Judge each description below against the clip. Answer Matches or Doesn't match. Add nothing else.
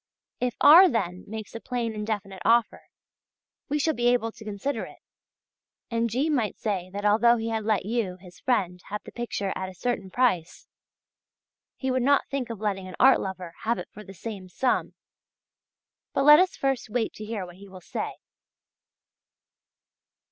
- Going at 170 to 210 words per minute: Matches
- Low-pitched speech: Doesn't match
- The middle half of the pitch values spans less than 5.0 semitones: Matches